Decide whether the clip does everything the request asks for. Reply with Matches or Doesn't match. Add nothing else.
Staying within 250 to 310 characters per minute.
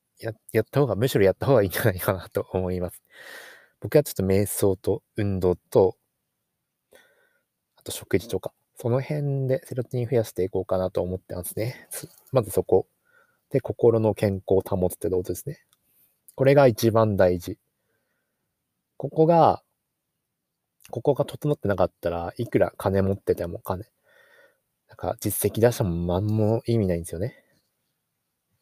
Matches